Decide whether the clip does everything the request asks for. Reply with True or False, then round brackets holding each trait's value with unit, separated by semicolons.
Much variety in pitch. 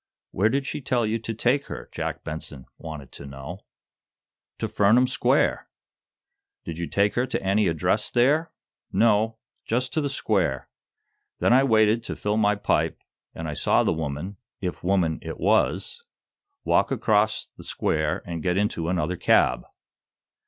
True (5.7 semitones)